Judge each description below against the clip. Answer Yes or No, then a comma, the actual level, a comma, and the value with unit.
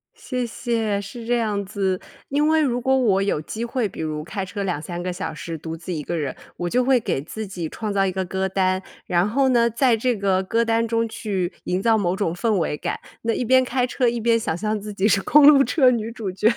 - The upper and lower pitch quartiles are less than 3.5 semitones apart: No, average, 4.2 semitones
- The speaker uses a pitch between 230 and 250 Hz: No, high, 210 Hz